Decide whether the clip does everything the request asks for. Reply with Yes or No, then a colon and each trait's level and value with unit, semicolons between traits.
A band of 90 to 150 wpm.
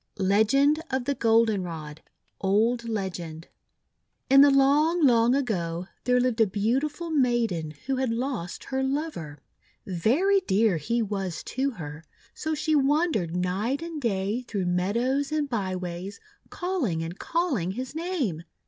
Yes: average, 140 wpm